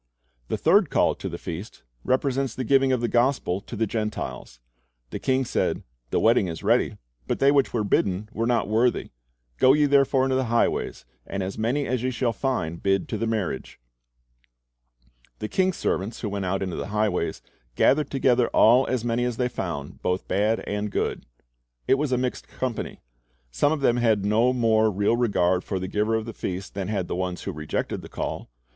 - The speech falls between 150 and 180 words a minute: No, average, 200 wpm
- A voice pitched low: Yes, low, 115 Hz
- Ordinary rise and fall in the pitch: Yes, average, 4.7 semitones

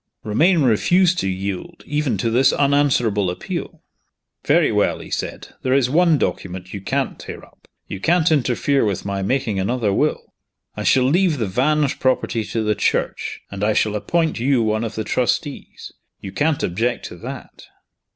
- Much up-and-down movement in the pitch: Yes, wide, 5.9 semitones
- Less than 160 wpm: No, average, 170 wpm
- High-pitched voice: No, low, 125 Hz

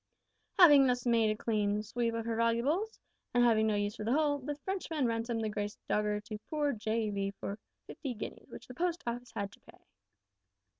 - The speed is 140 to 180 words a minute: No, average, 195 wpm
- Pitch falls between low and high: No, high, 230 Hz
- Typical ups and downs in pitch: Yes, average, 4.2 semitones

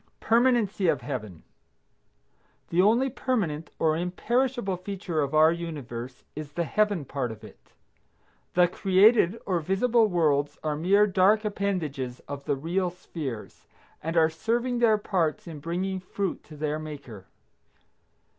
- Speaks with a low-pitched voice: No, medium, 170 Hz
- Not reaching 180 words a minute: Yes, slow, 135 wpm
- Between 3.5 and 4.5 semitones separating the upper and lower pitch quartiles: No, average, 5.3 semitones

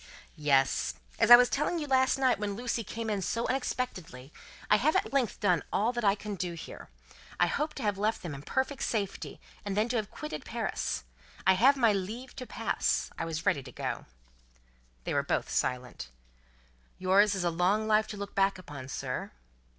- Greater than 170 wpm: Yes, average, 195 wpm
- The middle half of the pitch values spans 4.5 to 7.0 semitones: Yes, average, 5.1 semitones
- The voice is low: No, high, 210 Hz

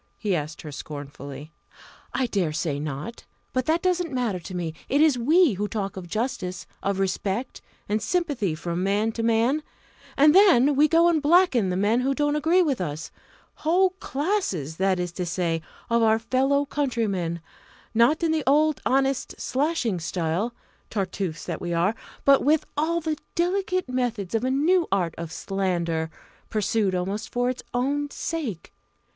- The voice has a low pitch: No, high, 230 Hz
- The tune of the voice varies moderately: No, wide, 8.3 semitones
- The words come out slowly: No, average, 165 wpm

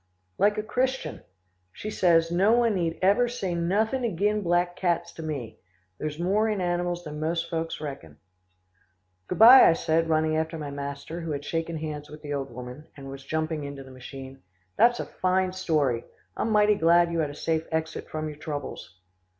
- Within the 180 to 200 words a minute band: Yes, average, 190 wpm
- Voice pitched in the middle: Yes, medium, 165 Hz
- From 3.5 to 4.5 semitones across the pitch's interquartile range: Yes, average, 3.9 semitones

